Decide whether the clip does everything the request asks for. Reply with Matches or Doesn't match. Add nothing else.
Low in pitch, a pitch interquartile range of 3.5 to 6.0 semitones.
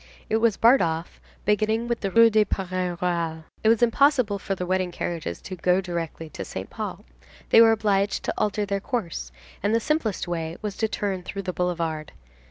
Doesn't match